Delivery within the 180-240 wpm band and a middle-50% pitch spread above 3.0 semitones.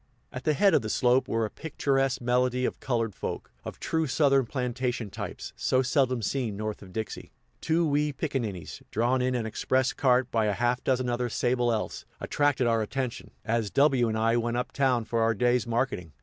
No: average, 195 wpm; narrow, 2.5 semitones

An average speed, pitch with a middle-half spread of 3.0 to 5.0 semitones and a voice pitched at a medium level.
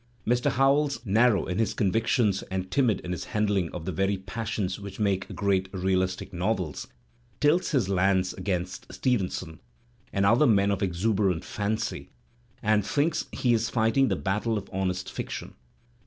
No: average, 155 wpm; average, 3.3 semitones; low, 100 Hz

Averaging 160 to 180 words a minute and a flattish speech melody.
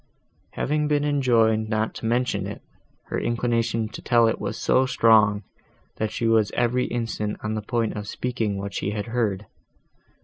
Yes: average, 170 wpm; narrow, 2.1 semitones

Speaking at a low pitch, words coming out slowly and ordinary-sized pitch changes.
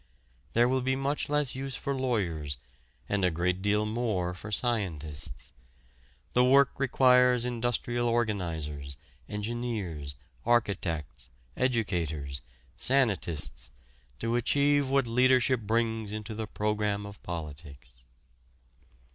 No: low, 110 Hz; slow, 105 wpm; wide, 6.2 semitones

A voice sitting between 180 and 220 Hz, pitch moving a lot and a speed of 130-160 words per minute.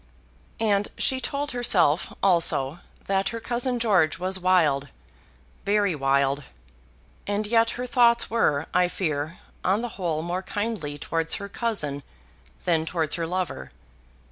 Yes: medium, 185 Hz; wide, 6.0 semitones; slow, 135 wpm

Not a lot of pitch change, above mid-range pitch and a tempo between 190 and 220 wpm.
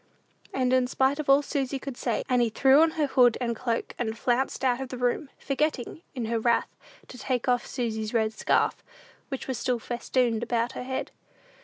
Yes: narrow, 2.1 semitones; very high, 250 Hz; average, 195 wpm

